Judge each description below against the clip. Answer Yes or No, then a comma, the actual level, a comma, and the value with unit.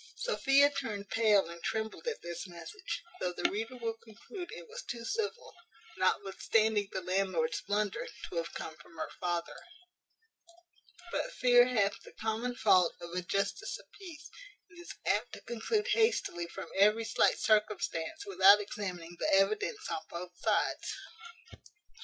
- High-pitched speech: Yes, high, 210 Hz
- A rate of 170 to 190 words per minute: No, average, 150 wpm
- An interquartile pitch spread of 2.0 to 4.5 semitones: No, wide, 5.5 semitones